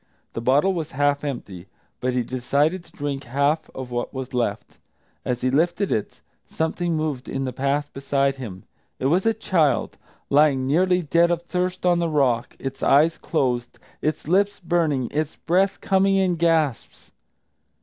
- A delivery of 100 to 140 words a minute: No, average, 165 wpm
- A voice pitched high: No, medium, 145 Hz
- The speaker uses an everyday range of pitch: Yes, average, 4.6 semitones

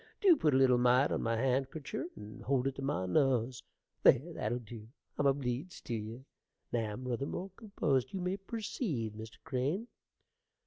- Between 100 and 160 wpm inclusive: No, average, 175 wpm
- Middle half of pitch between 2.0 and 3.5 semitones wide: No, average, 4.2 semitones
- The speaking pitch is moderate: No, low, 130 Hz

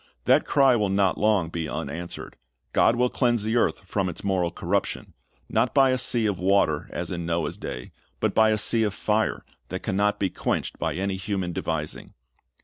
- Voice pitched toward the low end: Yes, low, 100 Hz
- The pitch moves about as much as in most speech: Yes, average, 4.1 semitones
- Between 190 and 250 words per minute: Yes, average, 195 wpm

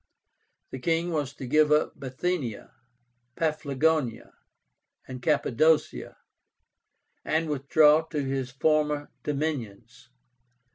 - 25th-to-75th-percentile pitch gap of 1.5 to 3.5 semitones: Yes, average, 3.1 semitones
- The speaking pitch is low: No, medium, 150 Hz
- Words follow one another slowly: Yes, slow, 90 wpm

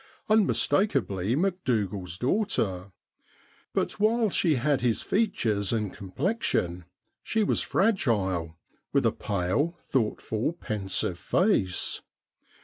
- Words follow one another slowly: Yes, slow, 100 wpm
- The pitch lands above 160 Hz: No, low, 115 Hz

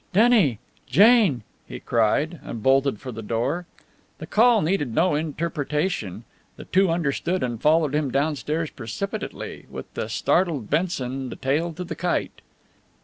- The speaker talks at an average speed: Yes, average, 145 wpm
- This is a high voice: No, medium, 150 Hz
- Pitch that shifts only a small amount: No, average, 5.3 semitones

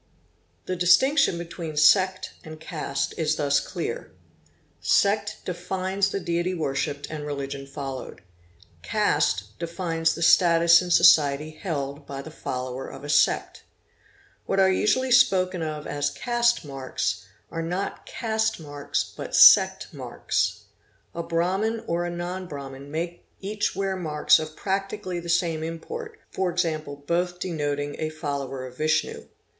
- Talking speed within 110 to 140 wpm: Yes, slow, 135 wpm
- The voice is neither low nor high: Yes, medium, 170 Hz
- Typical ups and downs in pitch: Yes, average, 4.2 semitones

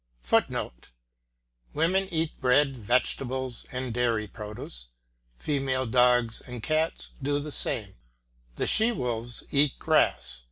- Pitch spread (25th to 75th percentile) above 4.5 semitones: No, average, 4.0 semitones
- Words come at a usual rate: No, slow, 115 wpm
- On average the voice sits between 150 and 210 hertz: No, low, 125 Hz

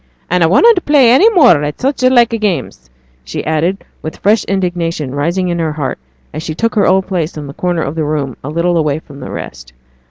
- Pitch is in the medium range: Yes, medium, 170 Hz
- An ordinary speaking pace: No, fast, 220 wpm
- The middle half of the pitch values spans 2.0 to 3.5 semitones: No, average, 5.1 semitones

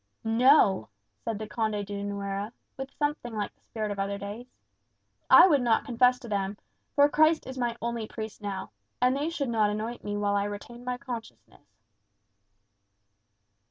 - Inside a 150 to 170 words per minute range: Yes, average, 165 wpm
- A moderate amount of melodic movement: Yes, average, 3.5 semitones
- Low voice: No, high, 225 Hz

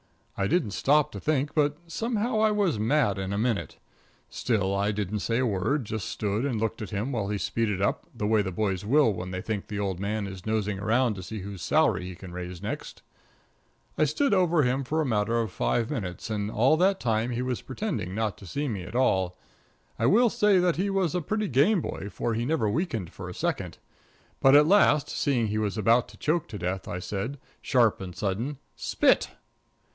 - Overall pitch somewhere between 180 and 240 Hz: No, low, 110 Hz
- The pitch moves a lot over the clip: Yes, wide, 6.5 semitones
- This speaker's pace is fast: Yes, fast, 215 wpm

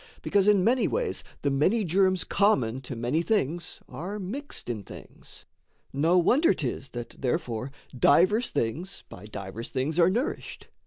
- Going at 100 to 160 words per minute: Yes, average, 150 wpm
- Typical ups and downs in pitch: No, wide, 7.9 semitones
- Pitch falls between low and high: Yes, medium, 170 Hz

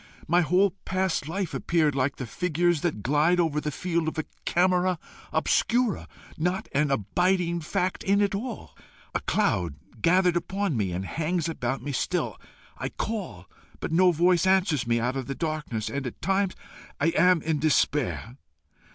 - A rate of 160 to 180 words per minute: Yes, average, 165 wpm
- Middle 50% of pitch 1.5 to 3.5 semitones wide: No, average, 4.3 semitones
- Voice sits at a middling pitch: Yes, medium, 165 Hz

